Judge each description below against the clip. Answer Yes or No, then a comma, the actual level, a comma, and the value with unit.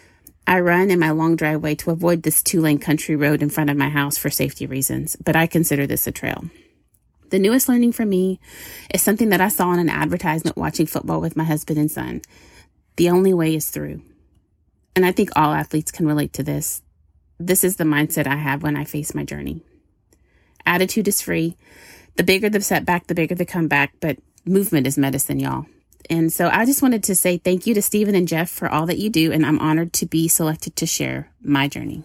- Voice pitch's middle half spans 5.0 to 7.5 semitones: No, average, 3.6 semitones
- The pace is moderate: No, fast, 215 wpm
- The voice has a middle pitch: Yes, medium, 160 Hz